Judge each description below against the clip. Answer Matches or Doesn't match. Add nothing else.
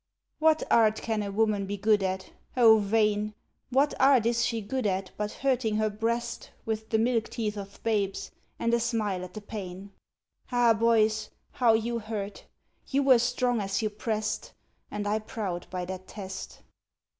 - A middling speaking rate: Matches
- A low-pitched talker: Doesn't match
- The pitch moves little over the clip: Matches